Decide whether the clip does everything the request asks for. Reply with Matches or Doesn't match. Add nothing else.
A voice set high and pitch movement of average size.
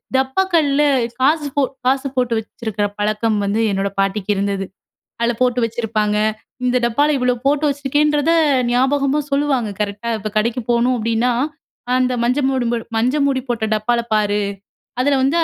Matches